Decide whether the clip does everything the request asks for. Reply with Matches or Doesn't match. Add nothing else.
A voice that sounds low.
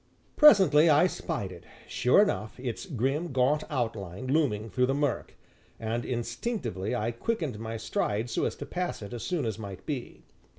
Matches